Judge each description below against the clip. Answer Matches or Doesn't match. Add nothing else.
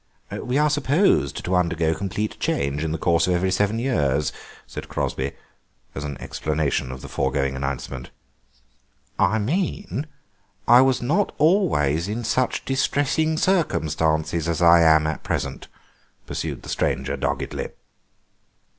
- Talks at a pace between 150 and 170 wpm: Doesn't match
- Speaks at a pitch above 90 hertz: Doesn't match